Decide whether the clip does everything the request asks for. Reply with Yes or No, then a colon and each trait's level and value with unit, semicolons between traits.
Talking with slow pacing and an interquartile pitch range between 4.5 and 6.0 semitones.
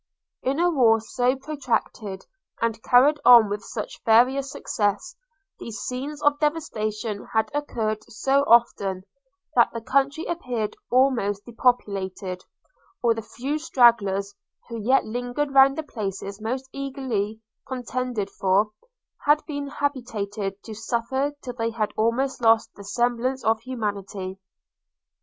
No: slow, 130 wpm; average, 4.0 semitones